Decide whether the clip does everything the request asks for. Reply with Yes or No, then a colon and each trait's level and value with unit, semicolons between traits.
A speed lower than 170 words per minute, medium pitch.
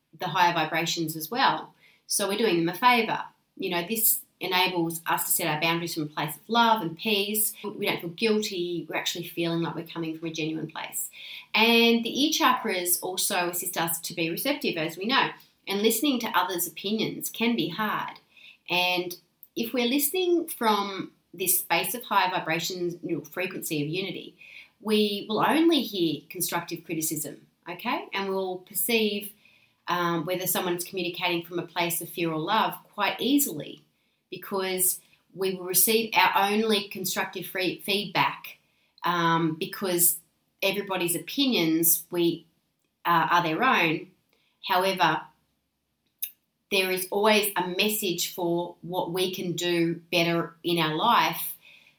Yes: average, 155 wpm; medium, 180 Hz